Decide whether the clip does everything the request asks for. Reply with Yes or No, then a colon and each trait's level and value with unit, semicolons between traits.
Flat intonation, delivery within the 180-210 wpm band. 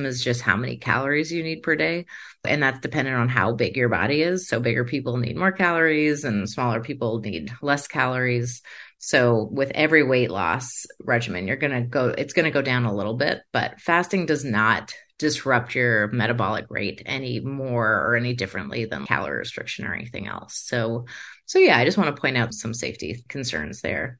No: average, 4.3 semitones; average, 200 wpm